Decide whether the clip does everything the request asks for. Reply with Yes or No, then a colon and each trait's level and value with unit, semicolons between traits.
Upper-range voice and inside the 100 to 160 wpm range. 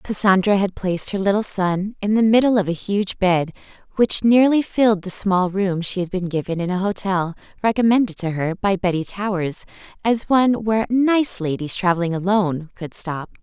No: high, 195 Hz; average, 185 wpm